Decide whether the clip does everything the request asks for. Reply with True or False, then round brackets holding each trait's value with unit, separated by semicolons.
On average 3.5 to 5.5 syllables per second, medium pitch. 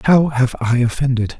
False (5.1 syllables/s; 130 Hz)